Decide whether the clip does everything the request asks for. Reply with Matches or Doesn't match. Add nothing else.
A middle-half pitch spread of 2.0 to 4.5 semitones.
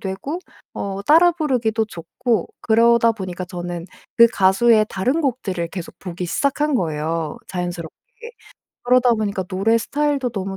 Doesn't match